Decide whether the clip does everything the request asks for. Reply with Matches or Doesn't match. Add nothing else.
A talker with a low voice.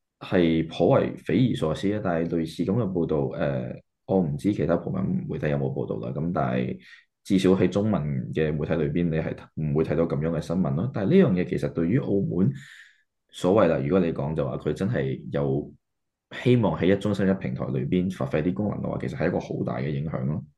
Matches